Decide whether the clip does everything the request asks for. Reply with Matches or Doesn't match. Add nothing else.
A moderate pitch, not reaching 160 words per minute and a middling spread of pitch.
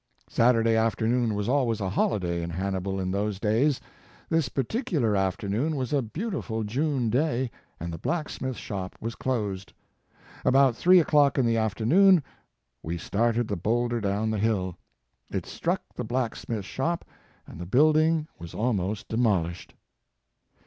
Doesn't match